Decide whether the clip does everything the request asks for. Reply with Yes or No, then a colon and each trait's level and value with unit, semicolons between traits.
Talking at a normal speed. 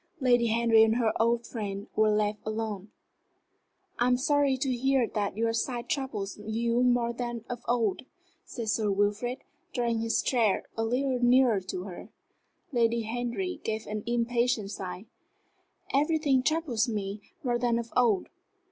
Yes: average, 150 wpm